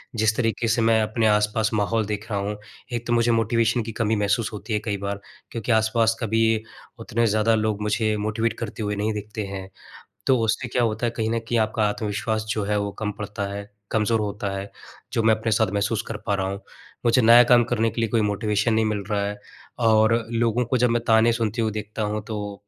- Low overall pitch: Yes, low, 110 Hz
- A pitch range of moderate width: No, narrow, 1.6 semitones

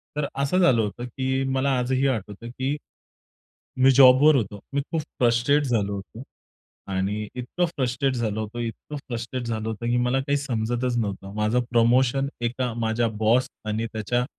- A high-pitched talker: No, low, 120 Hz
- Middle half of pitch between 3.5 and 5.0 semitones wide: No, average, 3.0 semitones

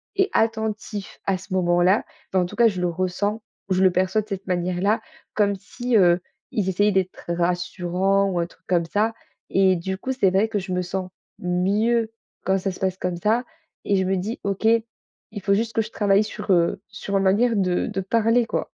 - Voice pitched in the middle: No, high, 195 Hz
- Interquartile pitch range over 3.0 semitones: No, average, 2.7 semitones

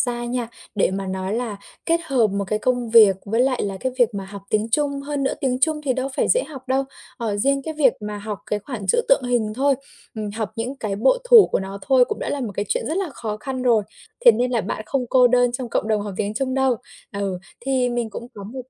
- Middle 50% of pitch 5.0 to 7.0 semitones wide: No, average, 4.1 semitones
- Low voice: No, high, 240 Hz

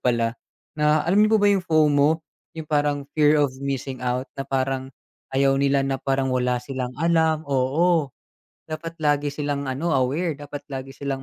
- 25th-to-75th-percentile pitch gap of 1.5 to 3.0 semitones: Yes, average, 2.7 semitones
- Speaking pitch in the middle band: Yes, medium, 145 Hz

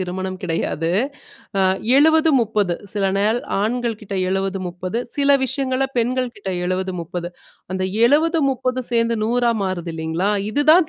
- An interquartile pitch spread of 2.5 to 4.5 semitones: No, wide, 5.6 semitones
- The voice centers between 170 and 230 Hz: Yes, high, 215 Hz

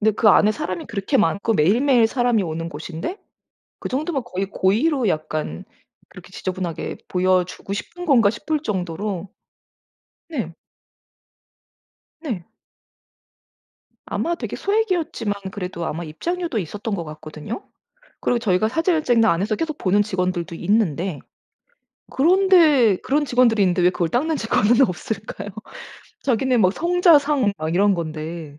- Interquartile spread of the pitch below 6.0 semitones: No, wide, 7.1 semitones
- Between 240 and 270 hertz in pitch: No, high, 210 Hz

